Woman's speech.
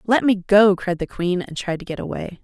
Yes: female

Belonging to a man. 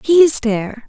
No: female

